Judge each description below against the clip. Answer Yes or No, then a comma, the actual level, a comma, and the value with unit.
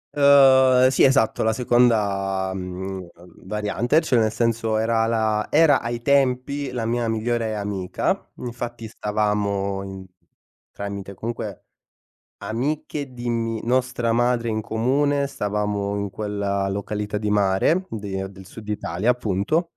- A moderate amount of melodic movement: Yes, average, 3.4 semitones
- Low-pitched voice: Yes, low, 110 Hz